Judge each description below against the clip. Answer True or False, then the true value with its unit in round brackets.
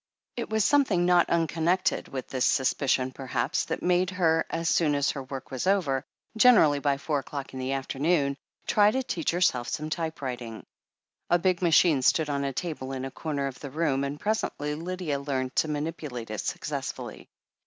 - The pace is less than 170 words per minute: False (185 wpm)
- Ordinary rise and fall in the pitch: True (4.5 semitones)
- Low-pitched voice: False (150 Hz)